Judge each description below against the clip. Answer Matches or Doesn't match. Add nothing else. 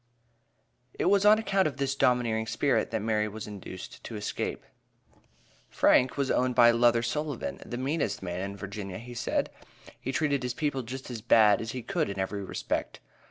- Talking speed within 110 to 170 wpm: Doesn't match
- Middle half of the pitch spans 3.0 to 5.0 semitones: Matches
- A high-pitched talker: Doesn't match